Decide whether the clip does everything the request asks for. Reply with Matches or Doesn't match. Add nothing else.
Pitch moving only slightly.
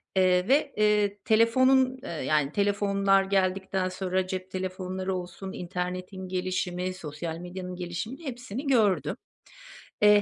Matches